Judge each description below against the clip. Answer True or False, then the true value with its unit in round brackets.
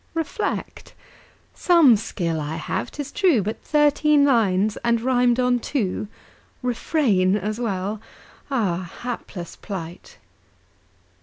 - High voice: True (225 Hz)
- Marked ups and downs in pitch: True (6.1 semitones)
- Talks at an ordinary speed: False (105 wpm)